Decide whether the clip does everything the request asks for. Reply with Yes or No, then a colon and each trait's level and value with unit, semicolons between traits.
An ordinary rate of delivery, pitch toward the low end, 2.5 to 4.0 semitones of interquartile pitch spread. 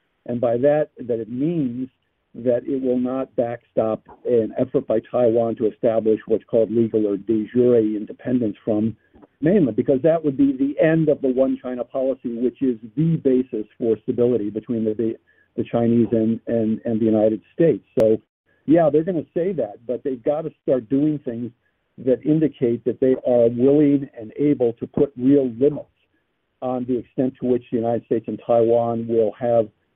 Yes: average, 185 wpm; low, 120 Hz; average, 2.8 semitones